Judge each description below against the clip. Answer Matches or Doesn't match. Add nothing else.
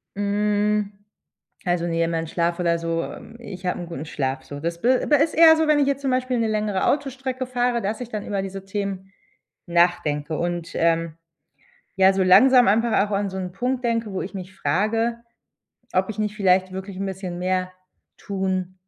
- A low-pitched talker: Doesn't match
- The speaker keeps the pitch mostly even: Doesn't match